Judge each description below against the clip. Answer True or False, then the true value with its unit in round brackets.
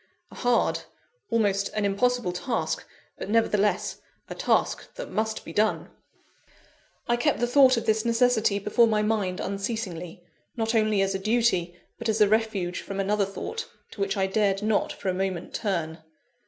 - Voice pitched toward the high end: True (210 Hz)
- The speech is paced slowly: False (170 wpm)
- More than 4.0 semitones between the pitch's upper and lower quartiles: False (2.8 semitones)